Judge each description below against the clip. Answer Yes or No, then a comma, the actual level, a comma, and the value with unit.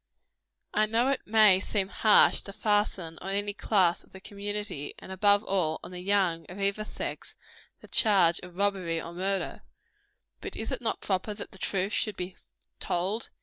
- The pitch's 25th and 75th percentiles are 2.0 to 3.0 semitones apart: Yes, narrow, 2.4 semitones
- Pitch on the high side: Yes, high, 200 Hz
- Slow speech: No, average, 180 wpm